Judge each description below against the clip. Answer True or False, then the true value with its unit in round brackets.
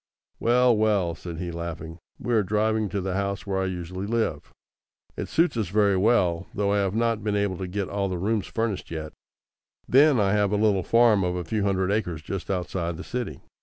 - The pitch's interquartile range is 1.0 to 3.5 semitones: True (3.2 semitones)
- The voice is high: False (100 Hz)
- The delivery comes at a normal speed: False (210 wpm)